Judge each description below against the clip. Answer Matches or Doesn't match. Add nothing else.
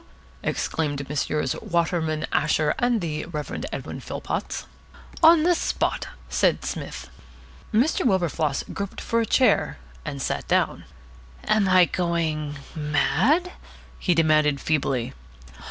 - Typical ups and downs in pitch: Doesn't match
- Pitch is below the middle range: Doesn't match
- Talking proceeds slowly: Matches